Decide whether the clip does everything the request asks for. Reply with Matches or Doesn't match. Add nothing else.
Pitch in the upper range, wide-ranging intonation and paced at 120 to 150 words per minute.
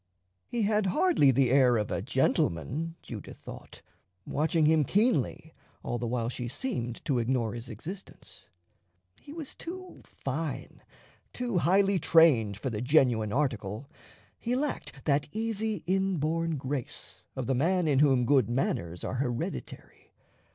Doesn't match